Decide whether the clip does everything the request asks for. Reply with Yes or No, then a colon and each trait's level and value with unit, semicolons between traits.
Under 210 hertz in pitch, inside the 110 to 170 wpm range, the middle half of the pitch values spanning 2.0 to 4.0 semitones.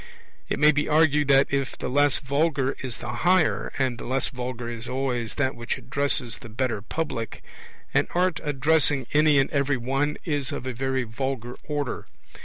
No: low, 135 Hz; average, 180 wpm; average, 2.8 semitones